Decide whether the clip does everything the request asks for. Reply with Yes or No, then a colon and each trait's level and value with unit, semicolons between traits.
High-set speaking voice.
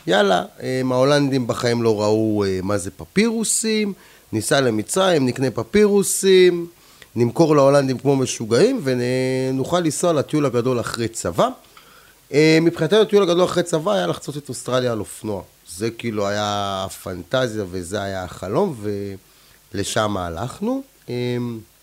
No: low, 130 Hz